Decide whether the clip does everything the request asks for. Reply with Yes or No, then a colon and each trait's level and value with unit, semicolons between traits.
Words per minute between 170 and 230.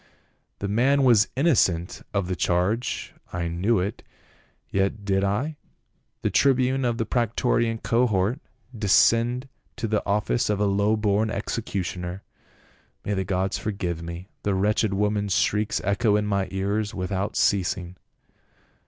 No: average, 145 wpm